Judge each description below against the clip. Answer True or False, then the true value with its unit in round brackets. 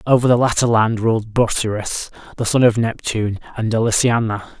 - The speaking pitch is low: True (115 Hz)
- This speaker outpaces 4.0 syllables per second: True (5.4 syllables/s)